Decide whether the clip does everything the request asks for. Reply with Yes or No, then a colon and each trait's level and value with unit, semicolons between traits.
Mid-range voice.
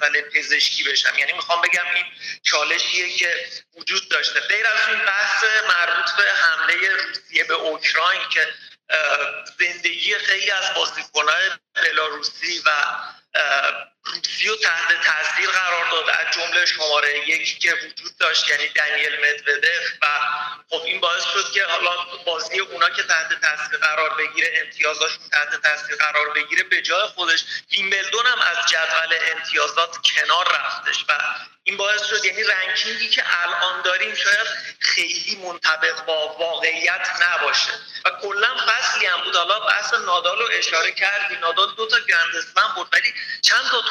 Yes: medium, 175 Hz